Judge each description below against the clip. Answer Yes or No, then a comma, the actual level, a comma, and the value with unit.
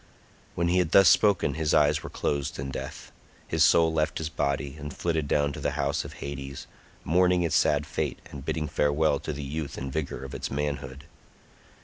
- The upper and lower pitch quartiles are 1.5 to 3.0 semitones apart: Yes, narrow, 2.4 semitones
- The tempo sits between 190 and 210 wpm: Yes, average, 200 wpm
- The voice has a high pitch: No, very low, 75 Hz